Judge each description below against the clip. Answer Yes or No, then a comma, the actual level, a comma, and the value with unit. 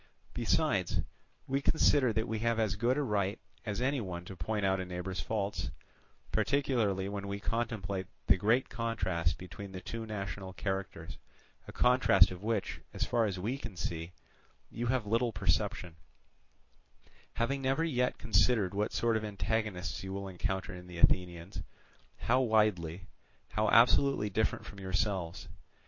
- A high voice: No, low, 105 Hz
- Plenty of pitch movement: No, average, 3.7 semitones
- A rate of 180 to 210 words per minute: No, average, 155 wpm